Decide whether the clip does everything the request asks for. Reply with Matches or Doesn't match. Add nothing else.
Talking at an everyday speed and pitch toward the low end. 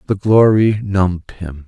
Matches